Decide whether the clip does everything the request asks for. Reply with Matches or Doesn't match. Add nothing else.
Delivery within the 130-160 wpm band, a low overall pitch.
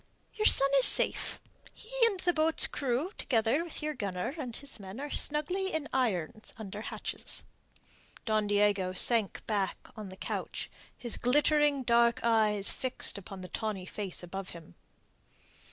Doesn't match